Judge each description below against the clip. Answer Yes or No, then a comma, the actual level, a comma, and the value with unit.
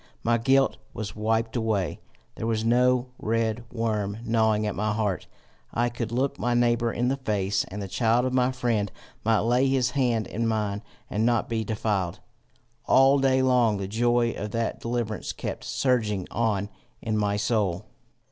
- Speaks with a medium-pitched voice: No, low, 115 Hz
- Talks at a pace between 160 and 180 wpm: Yes, average, 170 wpm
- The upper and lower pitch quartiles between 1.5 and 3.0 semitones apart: Yes, narrow, 2.4 semitones